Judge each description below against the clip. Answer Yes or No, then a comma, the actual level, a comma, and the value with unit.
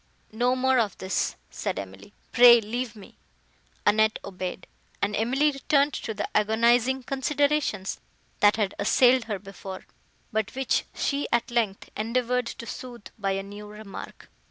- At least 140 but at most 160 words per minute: Yes, average, 150 wpm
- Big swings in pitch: No, average, 3.6 semitones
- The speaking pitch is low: No, high, 225 Hz